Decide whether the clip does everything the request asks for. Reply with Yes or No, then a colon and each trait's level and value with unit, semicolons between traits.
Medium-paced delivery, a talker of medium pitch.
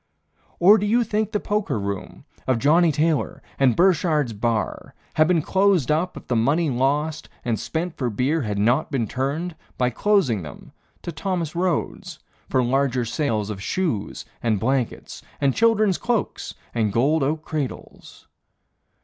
Yes: average, 155 wpm; medium, 145 Hz